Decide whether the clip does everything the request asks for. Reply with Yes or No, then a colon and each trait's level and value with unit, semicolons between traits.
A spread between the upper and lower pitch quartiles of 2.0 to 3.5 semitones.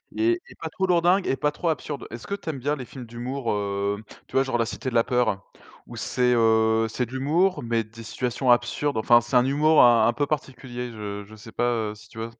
No: average, 4.1 semitones